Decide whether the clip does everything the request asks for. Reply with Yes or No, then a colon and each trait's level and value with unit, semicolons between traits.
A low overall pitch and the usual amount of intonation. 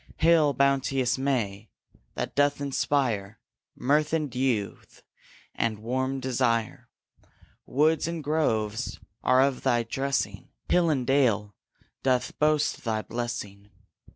Yes: low, 130 Hz; average, 3.7 semitones